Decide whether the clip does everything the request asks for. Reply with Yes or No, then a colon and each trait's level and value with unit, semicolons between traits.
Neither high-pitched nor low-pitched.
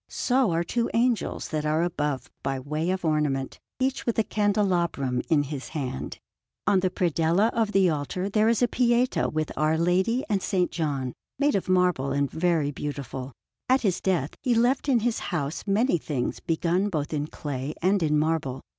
Yes: medium, 170 Hz